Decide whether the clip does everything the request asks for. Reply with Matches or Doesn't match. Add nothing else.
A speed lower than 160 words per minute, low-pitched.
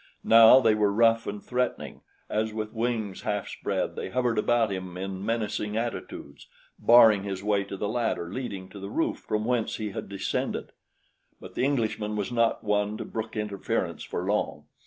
Doesn't match